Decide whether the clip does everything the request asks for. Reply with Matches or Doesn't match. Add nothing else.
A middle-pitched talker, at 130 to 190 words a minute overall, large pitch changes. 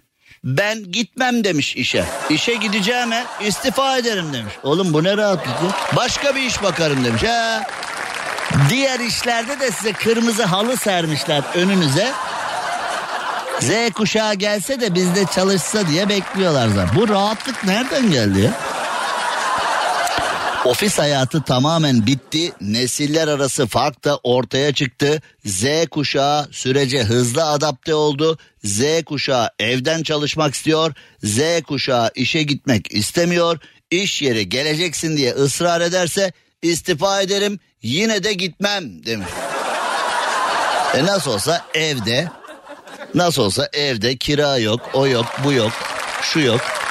Doesn't match